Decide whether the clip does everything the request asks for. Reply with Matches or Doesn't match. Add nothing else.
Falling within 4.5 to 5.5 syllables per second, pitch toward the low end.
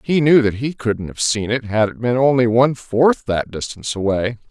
Matches